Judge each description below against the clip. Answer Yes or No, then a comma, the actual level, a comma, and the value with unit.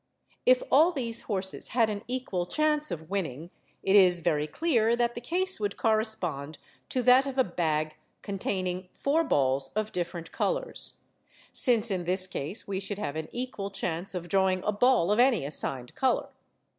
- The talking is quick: No, average, 170 wpm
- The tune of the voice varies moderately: No, wide, 6.1 semitones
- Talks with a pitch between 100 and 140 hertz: No, high, 200 Hz